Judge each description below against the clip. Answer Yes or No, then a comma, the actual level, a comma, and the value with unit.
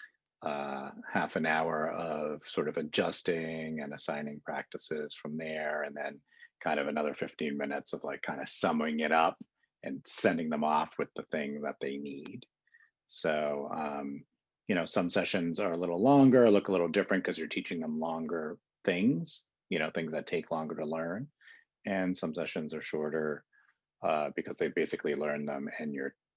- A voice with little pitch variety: Yes, narrow, 2.3 semitones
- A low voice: Yes, very low, 75 Hz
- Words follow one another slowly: No, average, 180 wpm